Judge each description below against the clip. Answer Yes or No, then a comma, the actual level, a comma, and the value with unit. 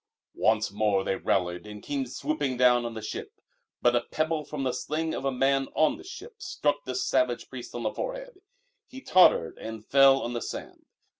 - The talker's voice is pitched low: Yes, low, 130 Hz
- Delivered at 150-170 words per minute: No, average, 200 wpm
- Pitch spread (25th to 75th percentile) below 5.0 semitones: No, average, 5.3 semitones